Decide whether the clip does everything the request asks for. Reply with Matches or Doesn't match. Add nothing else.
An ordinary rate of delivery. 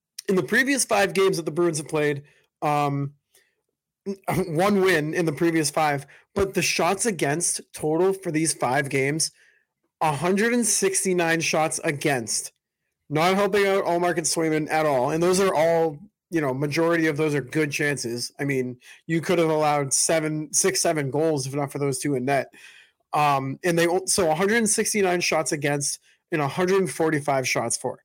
Matches